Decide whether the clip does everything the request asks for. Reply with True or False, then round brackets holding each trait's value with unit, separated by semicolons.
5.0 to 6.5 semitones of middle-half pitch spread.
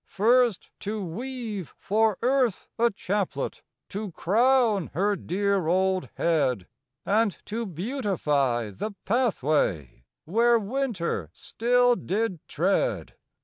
True (5.3 semitones)